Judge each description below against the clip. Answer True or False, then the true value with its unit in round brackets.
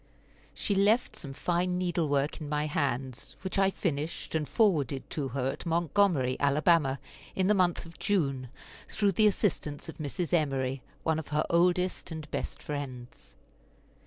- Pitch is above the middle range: False (160 Hz)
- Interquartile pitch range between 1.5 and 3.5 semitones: False (4.4 semitones)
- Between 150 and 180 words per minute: True (160 wpm)